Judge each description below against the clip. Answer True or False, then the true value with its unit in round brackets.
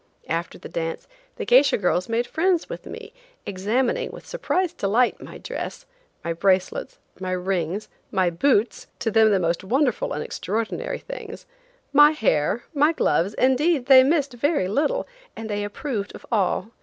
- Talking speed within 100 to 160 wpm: True (150 wpm)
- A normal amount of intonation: False (7.8 semitones)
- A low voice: False (230 Hz)